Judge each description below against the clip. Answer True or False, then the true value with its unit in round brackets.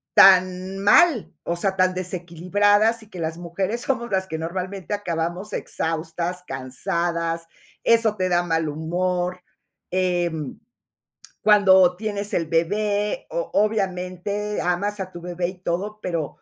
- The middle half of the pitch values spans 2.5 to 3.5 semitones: True (3.1 semitones)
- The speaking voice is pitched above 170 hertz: True (185 Hz)